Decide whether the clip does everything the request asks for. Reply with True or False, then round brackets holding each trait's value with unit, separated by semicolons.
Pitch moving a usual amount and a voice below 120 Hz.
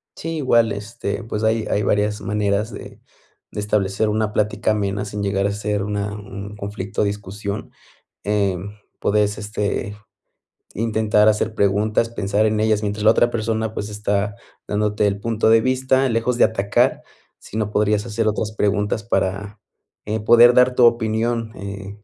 False (1.4 semitones; 105 Hz)